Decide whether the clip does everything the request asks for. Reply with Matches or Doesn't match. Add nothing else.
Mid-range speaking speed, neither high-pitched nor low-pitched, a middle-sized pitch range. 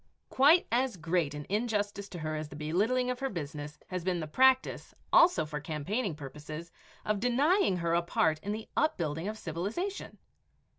Doesn't match